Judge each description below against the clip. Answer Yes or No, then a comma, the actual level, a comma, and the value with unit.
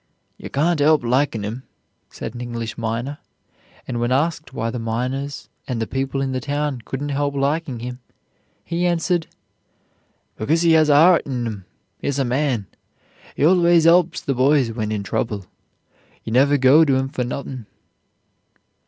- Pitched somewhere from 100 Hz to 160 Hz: Yes, low, 135 Hz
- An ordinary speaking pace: Yes, average, 165 wpm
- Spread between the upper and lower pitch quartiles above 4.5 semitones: No, average, 3.8 semitones